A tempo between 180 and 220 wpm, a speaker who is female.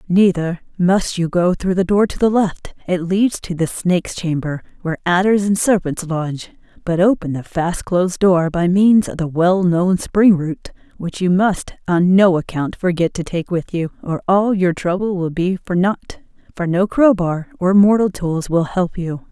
Yes: average, 195 wpm; female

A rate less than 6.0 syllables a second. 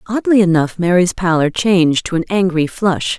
Yes: 5.0 syllables/s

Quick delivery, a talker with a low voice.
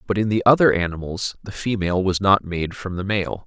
Yes: fast, 225 wpm; very low, 95 Hz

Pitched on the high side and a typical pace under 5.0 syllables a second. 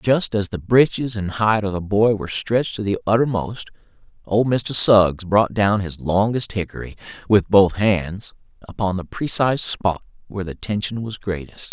No: low, 105 Hz; 4.7 syllables/s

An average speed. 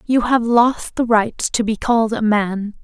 No: fast, 210 wpm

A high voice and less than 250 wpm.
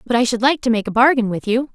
No: high, 240 Hz; fast, 345 wpm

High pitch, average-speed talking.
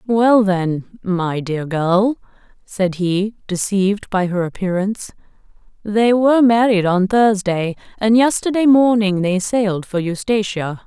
No: high, 200 Hz; slow, 125 wpm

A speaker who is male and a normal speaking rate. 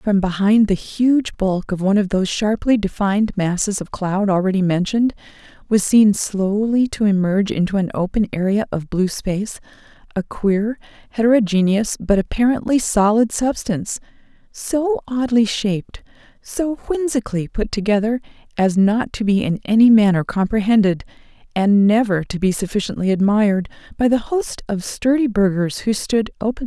No: female; average, 150 wpm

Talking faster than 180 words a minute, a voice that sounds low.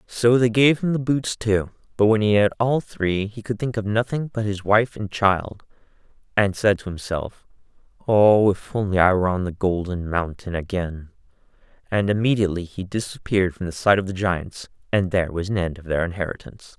Yes: average, 195 wpm; low, 100 Hz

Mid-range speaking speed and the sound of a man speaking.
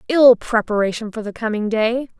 No: average, 165 wpm; female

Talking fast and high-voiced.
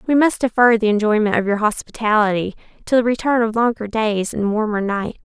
No: average, 195 wpm; high, 220 Hz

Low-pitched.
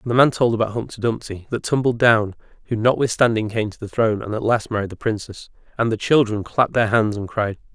Yes: low, 110 Hz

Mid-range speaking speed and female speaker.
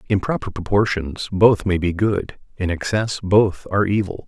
No: average, 170 wpm; male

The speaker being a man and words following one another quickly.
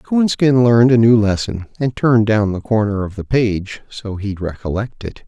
No: male; average, 195 wpm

